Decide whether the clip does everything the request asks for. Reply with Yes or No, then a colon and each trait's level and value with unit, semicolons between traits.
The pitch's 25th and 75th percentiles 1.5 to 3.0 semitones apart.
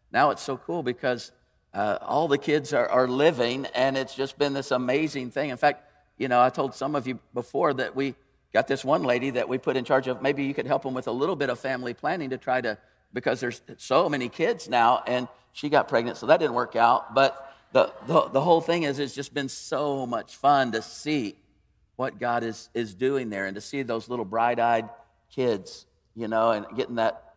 Yes: narrow, 2.5 semitones